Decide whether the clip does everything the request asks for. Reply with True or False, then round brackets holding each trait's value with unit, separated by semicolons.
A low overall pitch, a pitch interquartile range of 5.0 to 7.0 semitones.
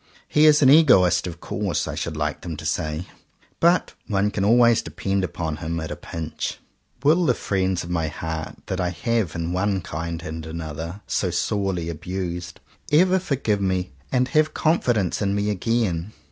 True (95 Hz; 5.5 semitones)